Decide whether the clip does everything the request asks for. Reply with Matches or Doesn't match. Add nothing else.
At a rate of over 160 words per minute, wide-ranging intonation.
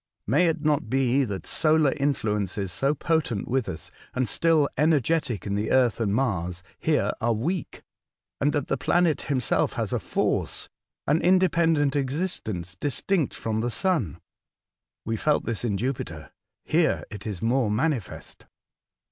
Doesn't match